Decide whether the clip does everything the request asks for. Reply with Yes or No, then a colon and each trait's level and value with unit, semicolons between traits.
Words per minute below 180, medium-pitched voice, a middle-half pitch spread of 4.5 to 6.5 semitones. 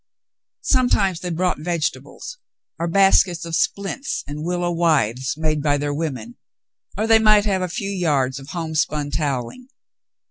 Yes: average, 150 wpm; medium, 165 Hz; average, 4.9 semitones